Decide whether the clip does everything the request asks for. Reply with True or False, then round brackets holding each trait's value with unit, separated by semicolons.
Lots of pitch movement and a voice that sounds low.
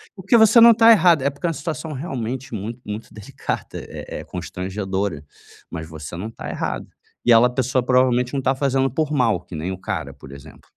True (6.7 semitones; 125 Hz)